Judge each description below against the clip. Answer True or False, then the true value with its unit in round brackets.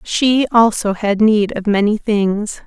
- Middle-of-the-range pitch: False (215 Hz)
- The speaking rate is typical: True (160 wpm)